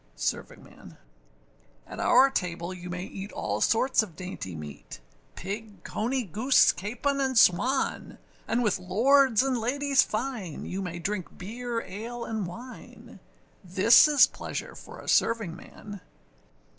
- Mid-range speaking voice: No, high, 215 Hz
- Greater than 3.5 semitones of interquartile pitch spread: Yes, wide, 5.5 semitones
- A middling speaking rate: No, slow, 130 wpm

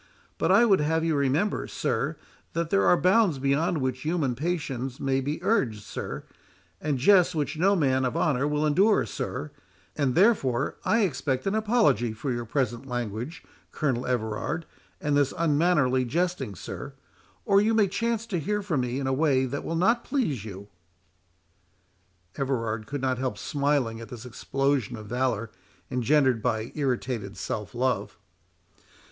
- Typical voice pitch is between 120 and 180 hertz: Yes, low, 135 Hz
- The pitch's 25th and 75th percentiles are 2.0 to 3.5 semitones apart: No, wide, 5.5 semitones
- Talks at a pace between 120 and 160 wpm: Yes, average, 155 wpm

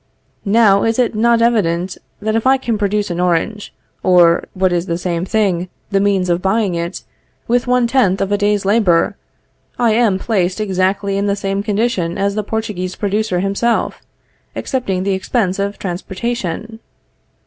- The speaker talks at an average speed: Yes, average, 170 wpm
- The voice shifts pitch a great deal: No, average, 3.2 semitones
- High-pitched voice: Yes, high, 200 Hz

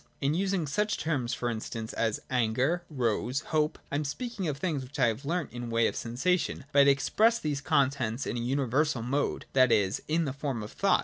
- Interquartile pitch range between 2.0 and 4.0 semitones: No, average, 4.4 semitones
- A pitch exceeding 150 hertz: No, medium, 140 Hz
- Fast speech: Yes, fast, 215 wpm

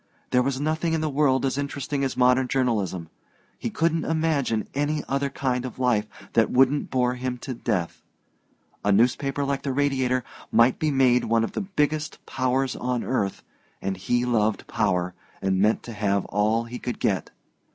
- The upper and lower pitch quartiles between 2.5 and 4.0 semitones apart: Yes, average, 3.7 semitones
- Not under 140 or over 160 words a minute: No, average, 175 wpm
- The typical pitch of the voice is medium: No, low, 125 Hz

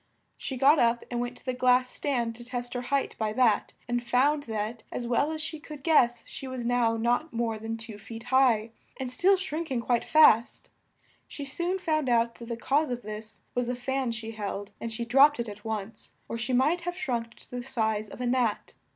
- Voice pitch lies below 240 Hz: No, high, 245 Hz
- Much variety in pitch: No, average, 2.8 semitones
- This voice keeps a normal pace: No, fast, 220 wpm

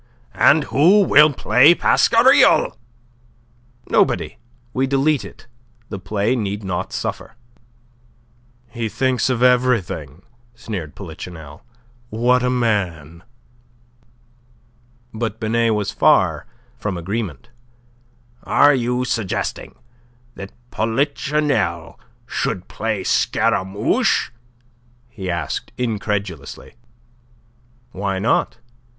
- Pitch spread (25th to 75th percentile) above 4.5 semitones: Yes, average, 4.9 semitones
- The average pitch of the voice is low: Yes, low, 110 Hz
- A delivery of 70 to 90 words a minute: Yes, slow, 85 wpm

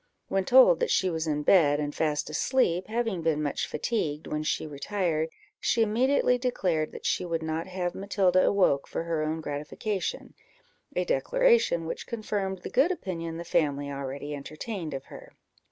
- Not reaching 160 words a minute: No, average, 170 wpm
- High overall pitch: No, medium, 170 Hz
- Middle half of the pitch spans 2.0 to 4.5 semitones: No, wide, 5.4 semitones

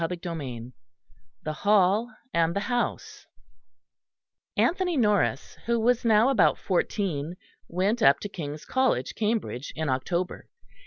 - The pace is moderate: No, slow, 120 wpm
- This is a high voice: Yes, high, 195 Hz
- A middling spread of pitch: No, wide, 6.3 semitones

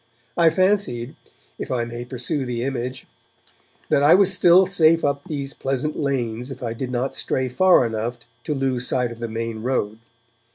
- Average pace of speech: Yes, average, 175 wpm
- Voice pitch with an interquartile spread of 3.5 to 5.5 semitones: Yes, average, 4.1 semitones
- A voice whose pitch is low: Yes, low, 130 Hz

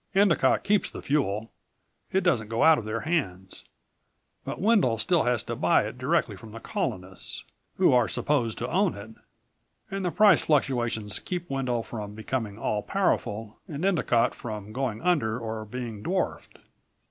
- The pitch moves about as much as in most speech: No, wide, 7.7 semitones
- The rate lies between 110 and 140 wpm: No, average, 160 wpm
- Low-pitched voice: Yes, low, 120 Hz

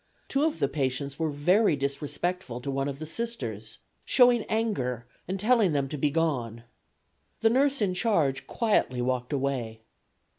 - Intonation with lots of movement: Yes, wide, 8.1 semitones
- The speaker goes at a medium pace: Yes, average, 150 wpm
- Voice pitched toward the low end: No, medium, 145 Hz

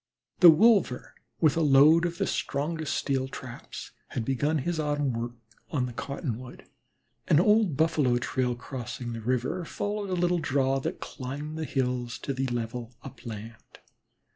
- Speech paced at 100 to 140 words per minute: No, average, 155 wpm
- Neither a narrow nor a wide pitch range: Yes, average, 4.3 semitones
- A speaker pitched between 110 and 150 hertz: Yes, low, 135 Hz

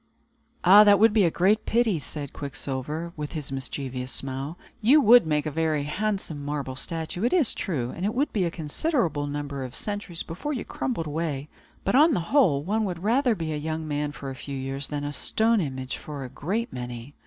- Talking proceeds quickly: Yes, fast, 210 wpm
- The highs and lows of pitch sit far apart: Yes, wide, 6.6 semitones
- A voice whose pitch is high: No, medium, 160 Hz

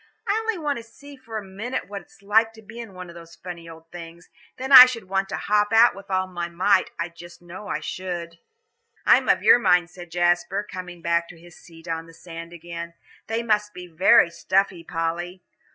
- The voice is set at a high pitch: No, medium, 180 Hz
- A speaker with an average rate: No, fast, 215 wpm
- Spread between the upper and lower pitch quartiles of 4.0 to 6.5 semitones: No, average, 3.6 semitones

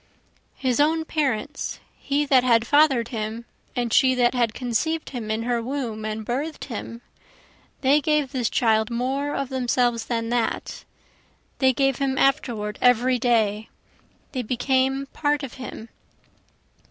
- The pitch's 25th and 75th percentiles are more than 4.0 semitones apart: No, average, 3.0 semitones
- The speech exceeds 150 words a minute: No, average, 140 wpm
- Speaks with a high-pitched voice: Yes, very high, 250 Hz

